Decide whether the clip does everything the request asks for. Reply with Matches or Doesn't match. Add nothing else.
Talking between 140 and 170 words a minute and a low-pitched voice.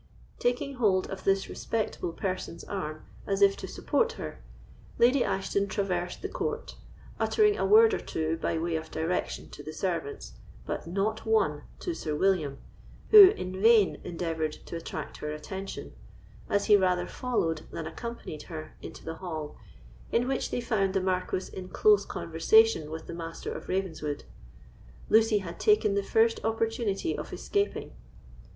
Doesn't match